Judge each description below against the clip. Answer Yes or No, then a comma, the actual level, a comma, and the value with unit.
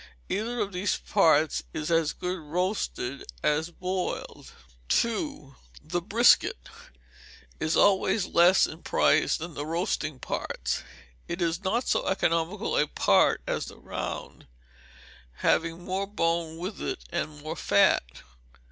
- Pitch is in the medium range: Yes, medium, 170 Hz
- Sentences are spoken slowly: Yes, slow, 130 wpm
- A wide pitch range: No, average, 3.6 semitones